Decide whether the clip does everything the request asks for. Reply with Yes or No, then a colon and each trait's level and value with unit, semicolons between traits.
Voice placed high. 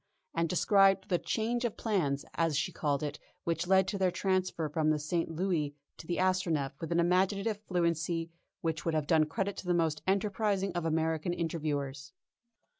No: medium, 170 Hz